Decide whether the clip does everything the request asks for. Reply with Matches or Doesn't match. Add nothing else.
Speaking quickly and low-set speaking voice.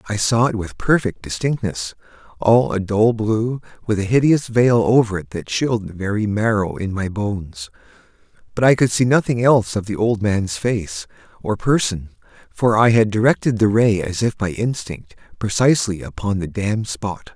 Doesn't match